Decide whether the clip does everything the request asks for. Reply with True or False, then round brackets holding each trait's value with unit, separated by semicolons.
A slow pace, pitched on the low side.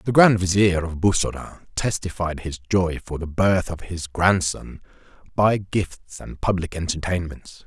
False (150 wpm; 90 Hz)